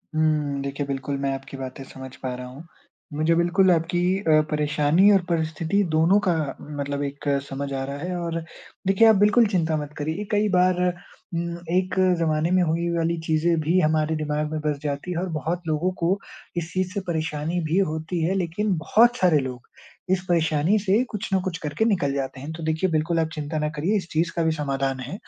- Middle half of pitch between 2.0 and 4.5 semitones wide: Yes, average, 3.3 semitones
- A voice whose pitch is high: No, medium, 160 Hz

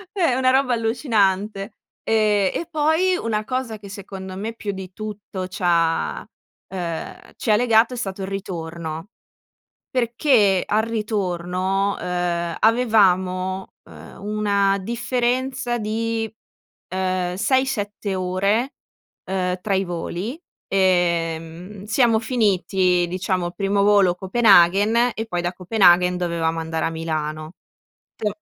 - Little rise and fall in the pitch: No, average, 3.7 semitones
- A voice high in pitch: Yes, high, 195 Hz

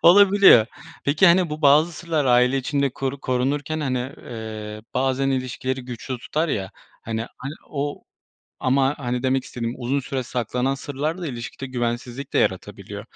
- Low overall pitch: Yes, low, 130 Hz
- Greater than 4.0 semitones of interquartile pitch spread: No, average, 2.8 semitones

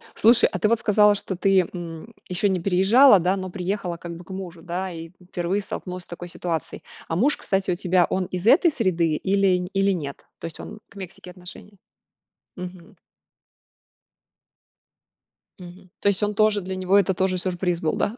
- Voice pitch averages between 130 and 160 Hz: No, medium, 185 Hz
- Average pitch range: No, narrow, 2.2 semitones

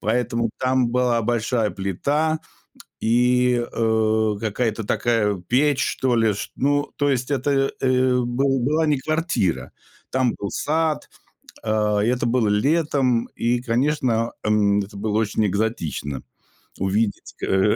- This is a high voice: No, low, 120 Hz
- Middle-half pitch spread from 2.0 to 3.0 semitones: No, average, 3.6 semitones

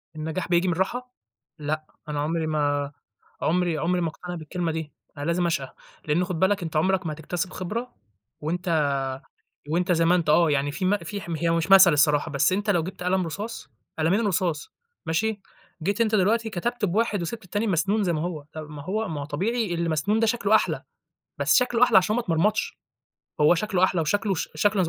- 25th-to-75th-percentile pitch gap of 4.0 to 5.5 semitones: Yes, average, 4.3 semitones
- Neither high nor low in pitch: Yes, medium, 175 Hz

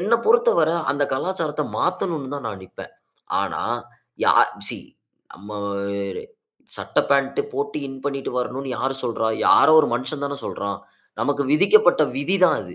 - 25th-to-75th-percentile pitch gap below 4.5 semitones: No, average, 5.0 semitones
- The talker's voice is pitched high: No, medium, 145 Hz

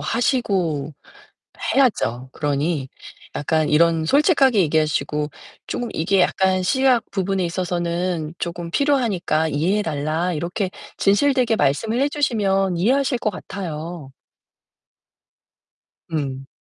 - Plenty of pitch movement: Yes, wide, 6.0 semitones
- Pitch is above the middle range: No, medium, 175 Hz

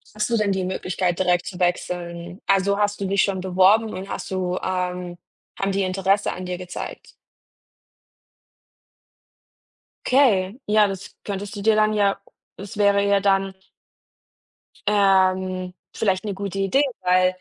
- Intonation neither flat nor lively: No, narrow, 1.7 semitones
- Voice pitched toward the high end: Yes, high, 195 Hz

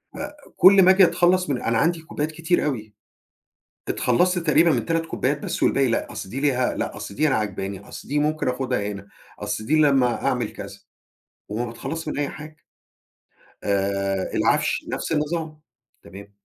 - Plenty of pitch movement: Yes, wide, 6.8 semitones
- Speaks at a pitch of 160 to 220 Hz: No, medium, 140 Hz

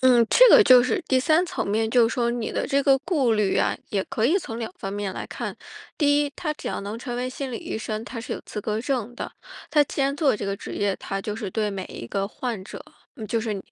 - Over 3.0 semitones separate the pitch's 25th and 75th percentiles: Yes, average, 4.4 semitones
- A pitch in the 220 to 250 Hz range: Yes, high, 235 Hz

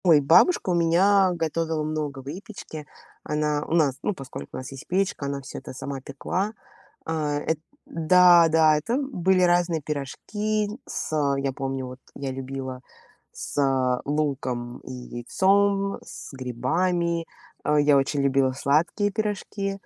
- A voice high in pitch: No, medium, 155 Hz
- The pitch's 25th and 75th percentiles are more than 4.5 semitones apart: Yes, average, 4.9 semitones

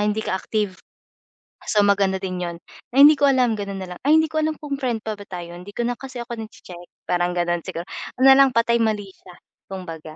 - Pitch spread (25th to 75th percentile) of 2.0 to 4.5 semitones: No, average, 5.2 semitones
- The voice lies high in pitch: Yes, high, 210 Hz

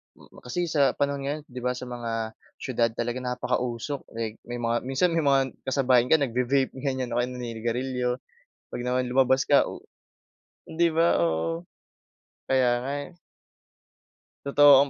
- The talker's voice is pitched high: No, low, 125 Hz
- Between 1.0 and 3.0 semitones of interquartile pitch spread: Yes, narrow, 2.5 semitones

